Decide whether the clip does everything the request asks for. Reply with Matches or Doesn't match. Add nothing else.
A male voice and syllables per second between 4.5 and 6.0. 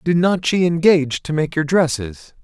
Matches